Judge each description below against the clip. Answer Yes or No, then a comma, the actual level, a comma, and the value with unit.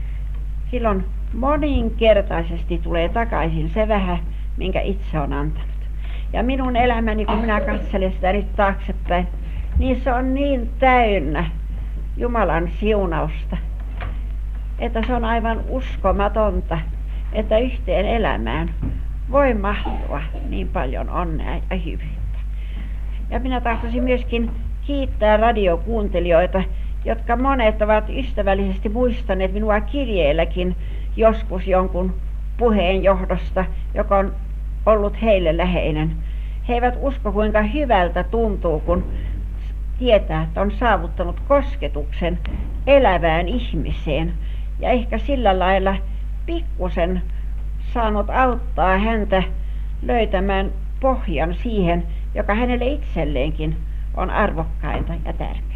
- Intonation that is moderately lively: No, wide, 5.7 semitones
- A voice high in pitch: Yes, high, 195 Hz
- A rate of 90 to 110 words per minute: Yes, average, 100 wpm